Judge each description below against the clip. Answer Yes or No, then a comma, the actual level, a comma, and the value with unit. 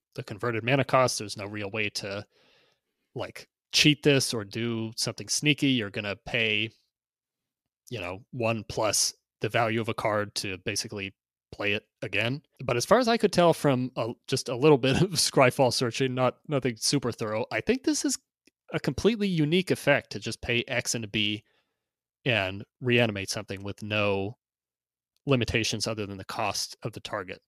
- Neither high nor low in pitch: No, low, 120 Hz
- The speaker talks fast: No, average, 180 wpm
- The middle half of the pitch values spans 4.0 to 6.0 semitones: Yes, average, 4.3 semitones